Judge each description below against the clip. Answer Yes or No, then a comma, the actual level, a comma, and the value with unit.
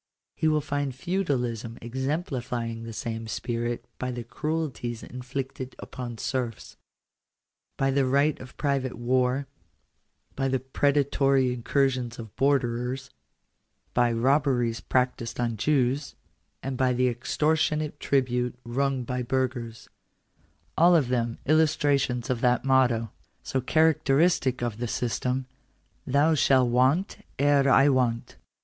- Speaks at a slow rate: Yes, slow, 125 wpm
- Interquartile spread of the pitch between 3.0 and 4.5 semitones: No, narrow, 2.5 semitones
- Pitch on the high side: No, low, 130 Hz